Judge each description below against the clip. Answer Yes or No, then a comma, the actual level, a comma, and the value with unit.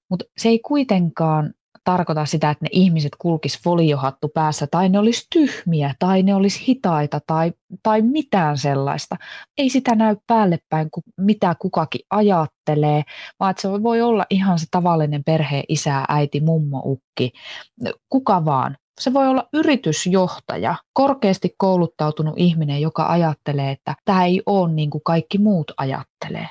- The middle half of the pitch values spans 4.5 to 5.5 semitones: Yes, average, 5.2 semitones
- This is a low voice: No, medium, 175 Hz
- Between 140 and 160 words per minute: Yes, average, 145 wpm